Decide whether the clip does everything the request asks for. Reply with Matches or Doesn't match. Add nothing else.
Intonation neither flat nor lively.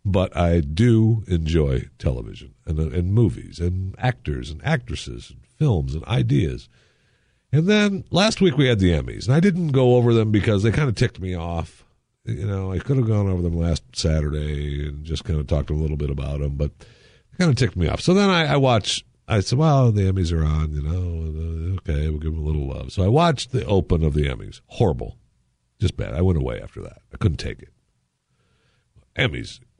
Doesn't match